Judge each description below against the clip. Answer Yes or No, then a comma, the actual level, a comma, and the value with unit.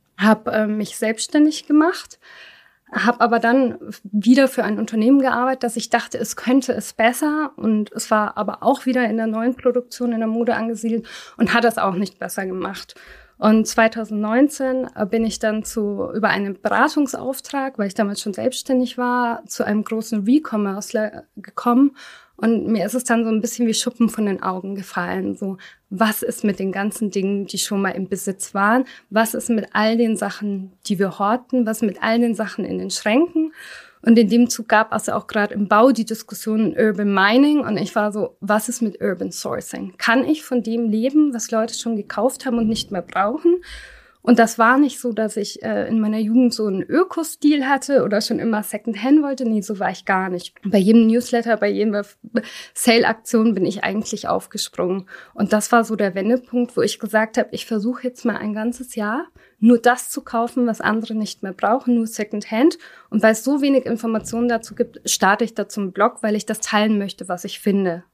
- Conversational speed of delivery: No, fast, 205 wpm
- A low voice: No, high, 225 Hz